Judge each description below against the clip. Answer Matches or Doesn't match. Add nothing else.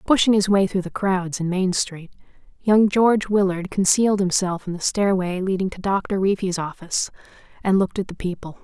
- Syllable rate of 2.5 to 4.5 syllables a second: Doesn't match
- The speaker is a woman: Matches